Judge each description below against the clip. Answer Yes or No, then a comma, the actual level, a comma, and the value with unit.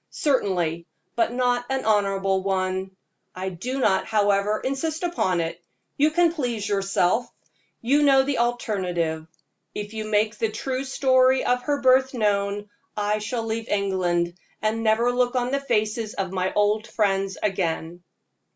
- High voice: Yes, high, 215 Hz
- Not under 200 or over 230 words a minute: No, average, 150 wpm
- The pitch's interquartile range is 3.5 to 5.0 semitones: Yes, average, 4.6 semitones